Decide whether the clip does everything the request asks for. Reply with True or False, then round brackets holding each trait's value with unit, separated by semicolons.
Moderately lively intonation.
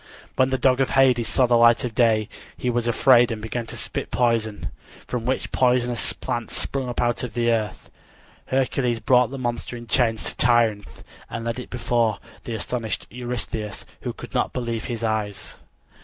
False (1.8 semitones)